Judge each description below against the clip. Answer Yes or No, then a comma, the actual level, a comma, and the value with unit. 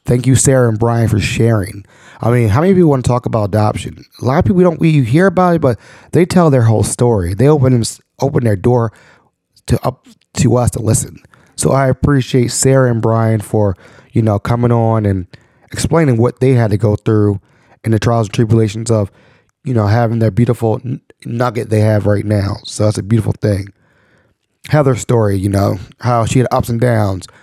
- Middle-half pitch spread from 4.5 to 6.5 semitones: No, average, 3.3 semitones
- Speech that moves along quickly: Yes, fast, 210 wpm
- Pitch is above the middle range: No, low, 120 Hz